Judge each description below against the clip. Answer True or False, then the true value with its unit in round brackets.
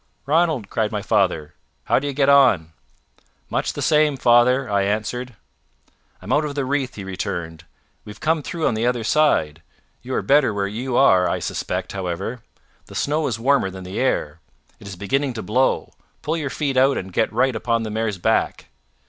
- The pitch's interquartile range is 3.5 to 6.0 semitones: True (5.6 semitones)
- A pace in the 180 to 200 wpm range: True (190 wpm)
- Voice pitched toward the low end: True (120 Hz)